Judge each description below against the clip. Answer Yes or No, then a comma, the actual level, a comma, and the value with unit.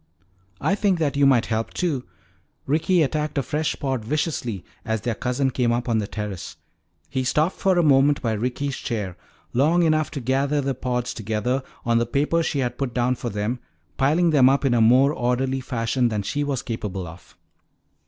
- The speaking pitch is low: Yes, low, 130 Hz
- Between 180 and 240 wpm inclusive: Yes, average, 190 wpm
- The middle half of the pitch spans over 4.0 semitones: No, average, 3.6 semitones